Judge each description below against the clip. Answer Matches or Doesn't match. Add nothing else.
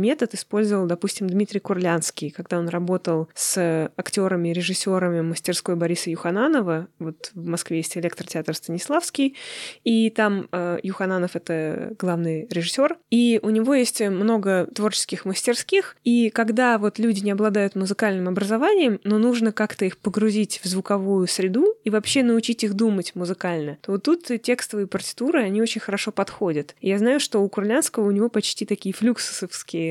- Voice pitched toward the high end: Matches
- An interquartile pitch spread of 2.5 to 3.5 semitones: Doesn't match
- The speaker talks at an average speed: Matches